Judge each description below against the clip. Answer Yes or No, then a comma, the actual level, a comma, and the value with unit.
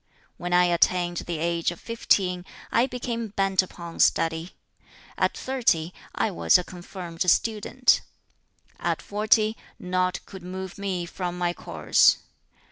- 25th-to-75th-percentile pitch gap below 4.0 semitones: Yes, average, 2.9 semitones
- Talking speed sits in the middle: No, slow, 130 wpm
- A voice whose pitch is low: No, medium, 180 Hz